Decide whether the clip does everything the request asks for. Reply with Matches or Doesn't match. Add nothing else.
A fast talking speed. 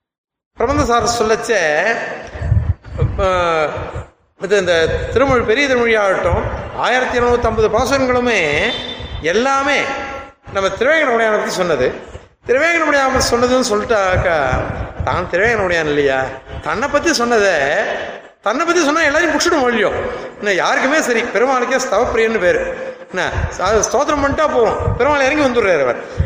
Doesn't match